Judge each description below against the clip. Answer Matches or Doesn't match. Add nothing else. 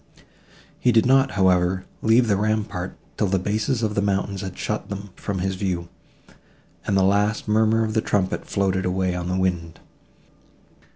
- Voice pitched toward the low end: Matches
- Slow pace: Doesn't match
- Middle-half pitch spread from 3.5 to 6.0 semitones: Doesn't match